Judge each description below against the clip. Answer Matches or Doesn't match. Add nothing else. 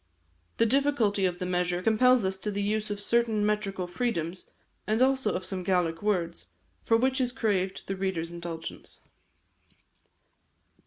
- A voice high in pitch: Matches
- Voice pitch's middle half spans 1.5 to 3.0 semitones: Doesn't match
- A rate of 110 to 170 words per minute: Matches